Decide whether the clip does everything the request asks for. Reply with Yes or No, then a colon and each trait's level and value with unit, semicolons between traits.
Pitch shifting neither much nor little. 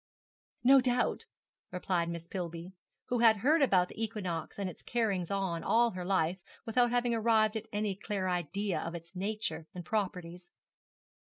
Yes: average, 4.1 semitones